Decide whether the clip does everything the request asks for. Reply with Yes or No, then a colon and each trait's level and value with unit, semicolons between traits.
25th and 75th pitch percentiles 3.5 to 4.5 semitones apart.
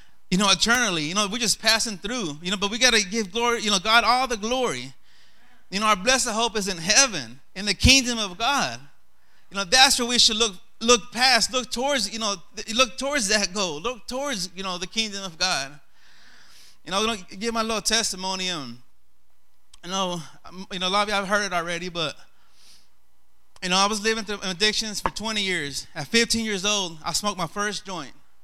Yes: average, 3.8 semitones